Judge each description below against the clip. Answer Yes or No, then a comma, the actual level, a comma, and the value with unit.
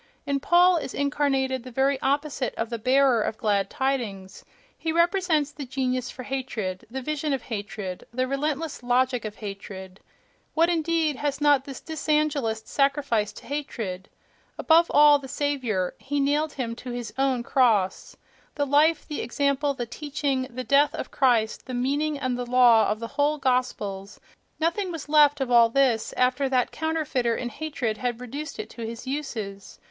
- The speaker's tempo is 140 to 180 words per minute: Yes, average, 165 wpm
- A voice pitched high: Yes, very high, 265 Hz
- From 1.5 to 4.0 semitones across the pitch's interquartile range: Yes, average, 3.7 semitones